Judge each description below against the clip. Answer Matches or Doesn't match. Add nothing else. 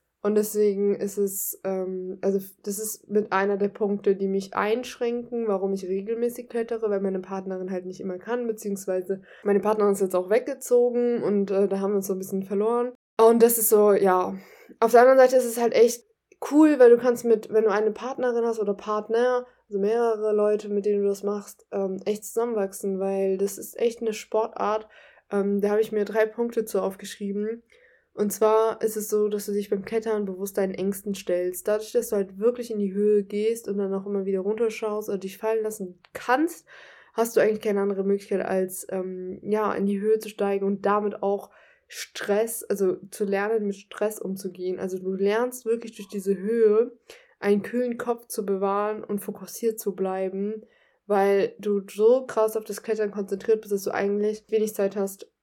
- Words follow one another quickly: Matches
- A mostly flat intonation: Matches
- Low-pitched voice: Doesn't match